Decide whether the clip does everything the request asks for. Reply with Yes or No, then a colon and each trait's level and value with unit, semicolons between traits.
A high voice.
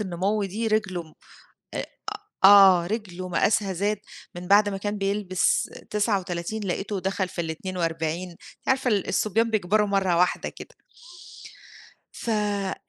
Yes: high, 195 Hz